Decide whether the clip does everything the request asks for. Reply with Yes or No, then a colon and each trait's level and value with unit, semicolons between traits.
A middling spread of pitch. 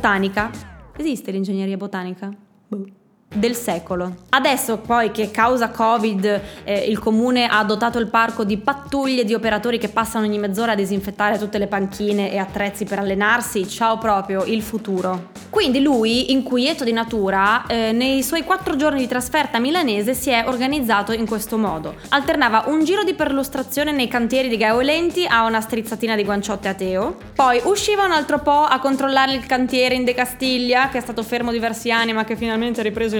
Yes: average, 3.8 semitones